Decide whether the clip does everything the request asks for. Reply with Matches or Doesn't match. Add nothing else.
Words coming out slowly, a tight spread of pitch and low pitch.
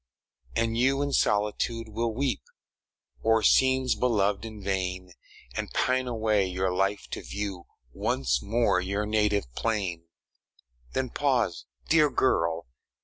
Doesn't match